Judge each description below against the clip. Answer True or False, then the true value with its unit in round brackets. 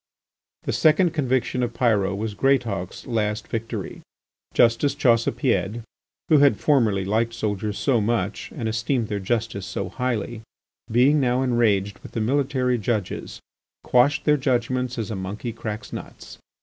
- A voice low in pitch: True (115 Hz)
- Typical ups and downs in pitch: True (3.3 semitones)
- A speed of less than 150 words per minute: True (140 wpm)